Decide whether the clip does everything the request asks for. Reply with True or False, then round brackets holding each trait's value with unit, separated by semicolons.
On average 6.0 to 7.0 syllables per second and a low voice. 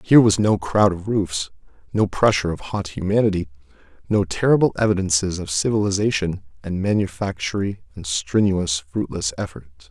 False (5.2 syllables/s; 95 Hz)